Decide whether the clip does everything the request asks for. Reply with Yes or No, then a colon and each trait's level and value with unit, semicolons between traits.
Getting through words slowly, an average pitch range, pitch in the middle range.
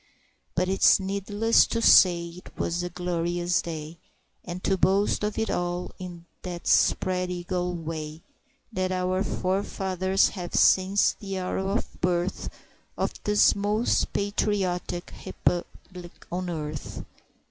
No: slow, 125 wpm; narrow, 1.8 semitones; medium, 180 Hz